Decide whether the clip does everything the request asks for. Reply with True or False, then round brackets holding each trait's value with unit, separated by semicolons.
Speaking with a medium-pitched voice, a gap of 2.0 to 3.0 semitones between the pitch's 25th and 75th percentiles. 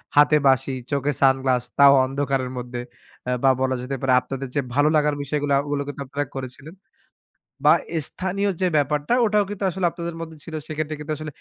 True (145 Hz; 2.7 semitones)